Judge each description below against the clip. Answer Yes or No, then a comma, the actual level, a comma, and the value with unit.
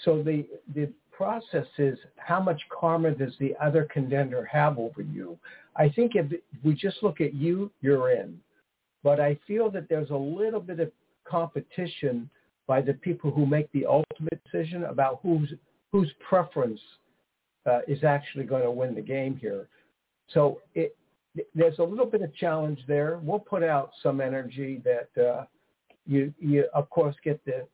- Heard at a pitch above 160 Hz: No, medium, 150 Hz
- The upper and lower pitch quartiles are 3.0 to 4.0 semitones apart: Yes, average, 3.6 semitones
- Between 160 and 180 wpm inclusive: Yes, average, 170 wpm